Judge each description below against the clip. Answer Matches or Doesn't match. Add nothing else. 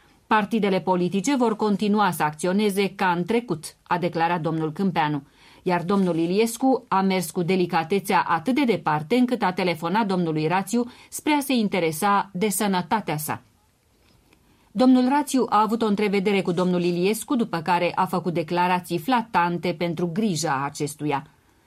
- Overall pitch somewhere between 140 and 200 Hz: Matches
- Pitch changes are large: Doesn't match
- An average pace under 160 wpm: Matches